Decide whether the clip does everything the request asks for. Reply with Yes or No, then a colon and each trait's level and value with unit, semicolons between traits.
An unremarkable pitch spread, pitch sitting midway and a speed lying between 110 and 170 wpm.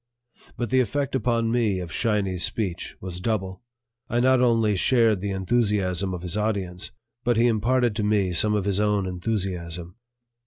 No: average, 3.9 semitones; low, 105 Hz; average, 165 wpm